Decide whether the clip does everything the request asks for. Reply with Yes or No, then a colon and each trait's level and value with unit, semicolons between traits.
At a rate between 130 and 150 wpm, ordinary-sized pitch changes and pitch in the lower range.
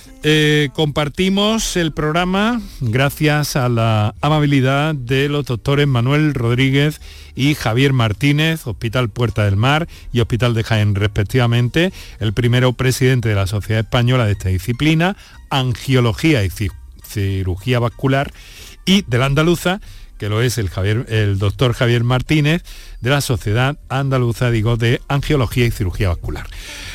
Yes: average, 140 wpm; average, 4.8 semitones; low, 125 Hz